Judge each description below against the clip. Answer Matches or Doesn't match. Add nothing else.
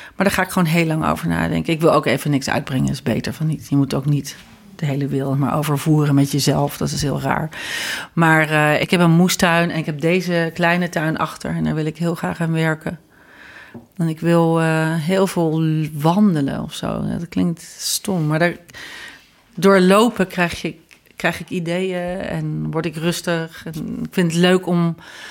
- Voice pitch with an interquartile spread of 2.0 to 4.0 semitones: Matches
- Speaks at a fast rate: Matches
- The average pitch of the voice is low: Doesn't match